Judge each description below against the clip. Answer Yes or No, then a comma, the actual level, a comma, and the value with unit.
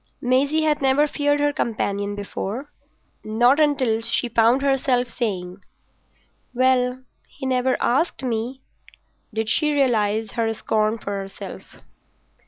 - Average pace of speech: No, slow, 120 wpm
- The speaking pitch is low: No, high, 245 Hz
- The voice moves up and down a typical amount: Yes, average, 3.6 semitones